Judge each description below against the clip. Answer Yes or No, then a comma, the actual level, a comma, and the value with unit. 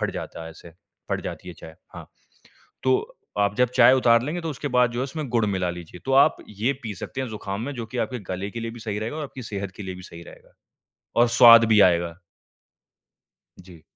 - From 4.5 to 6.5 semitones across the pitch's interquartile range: Yes, average, 5.2 semitones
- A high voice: No, low, 110 Hz